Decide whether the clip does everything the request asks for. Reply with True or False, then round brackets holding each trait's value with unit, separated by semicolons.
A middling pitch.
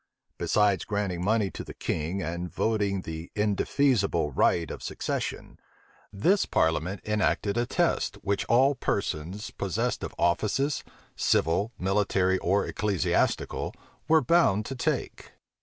False (100 Hz)